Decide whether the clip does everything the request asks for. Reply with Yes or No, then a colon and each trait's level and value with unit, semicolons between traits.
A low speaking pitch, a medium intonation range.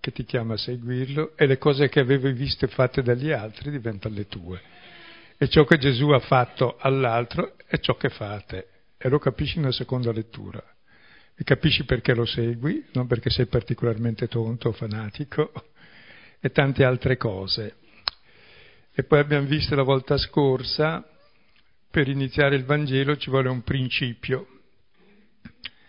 Yes: low, 130 Hz; average, 3.6 semitones